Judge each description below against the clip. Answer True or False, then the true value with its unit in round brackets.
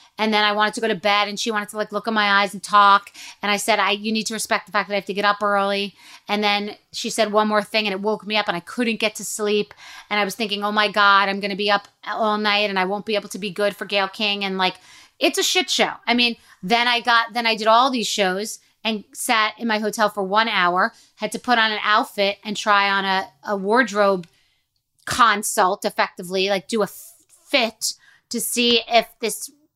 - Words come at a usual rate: False (255 wpm)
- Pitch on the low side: False (210 Hz)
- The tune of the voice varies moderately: False (1.8 semitones)